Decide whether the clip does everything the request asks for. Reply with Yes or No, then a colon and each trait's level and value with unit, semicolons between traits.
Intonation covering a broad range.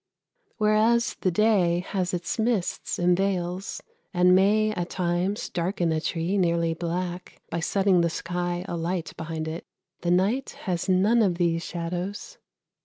No: narrow, 2.5 semitones